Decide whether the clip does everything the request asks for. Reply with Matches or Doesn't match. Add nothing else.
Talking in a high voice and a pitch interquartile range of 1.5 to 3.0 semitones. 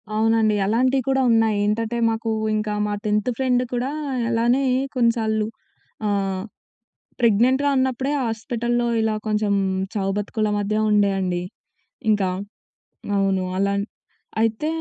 Matches